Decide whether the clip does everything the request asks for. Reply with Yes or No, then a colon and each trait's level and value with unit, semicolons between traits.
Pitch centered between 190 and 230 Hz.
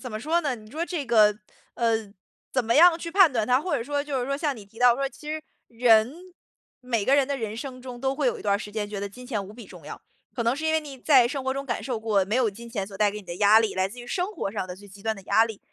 No: high, 240 Hz